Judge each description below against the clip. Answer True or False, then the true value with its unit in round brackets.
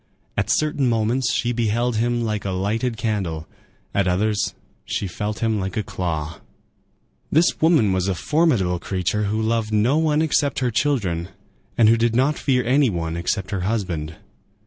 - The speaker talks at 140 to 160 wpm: False (170 wpm)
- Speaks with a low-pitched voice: True (110 Hz)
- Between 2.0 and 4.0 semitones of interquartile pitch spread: False (4.7 semitones)